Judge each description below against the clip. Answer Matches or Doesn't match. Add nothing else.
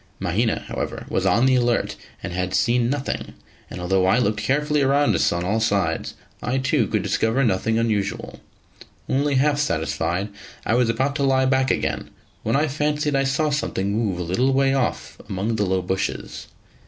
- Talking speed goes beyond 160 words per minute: Matches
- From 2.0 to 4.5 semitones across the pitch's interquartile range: Doesn't match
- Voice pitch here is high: Doesn't match